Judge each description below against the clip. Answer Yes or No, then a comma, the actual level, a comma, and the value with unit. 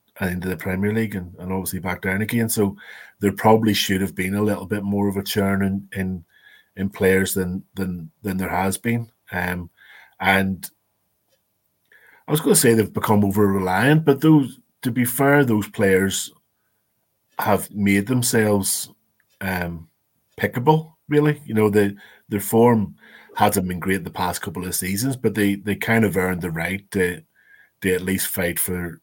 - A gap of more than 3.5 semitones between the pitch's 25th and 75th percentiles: No, average, 2.8 semitones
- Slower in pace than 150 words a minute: No, average, 180 wpm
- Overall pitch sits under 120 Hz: Yes, low, 100 Hz